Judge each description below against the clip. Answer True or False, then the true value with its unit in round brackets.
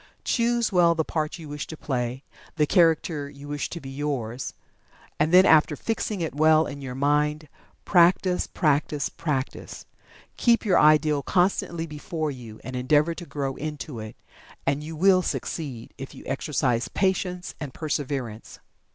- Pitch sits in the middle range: True (150 Hz)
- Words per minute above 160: False (155 wpm)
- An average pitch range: True (3.5 semitones)